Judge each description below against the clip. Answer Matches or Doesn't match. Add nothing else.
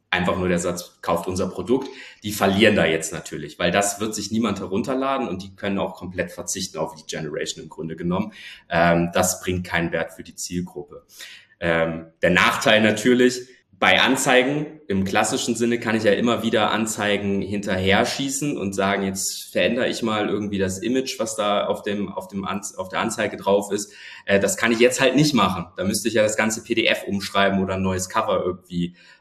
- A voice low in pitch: Matches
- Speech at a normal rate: Doesn't match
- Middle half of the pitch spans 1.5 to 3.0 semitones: Doesn't match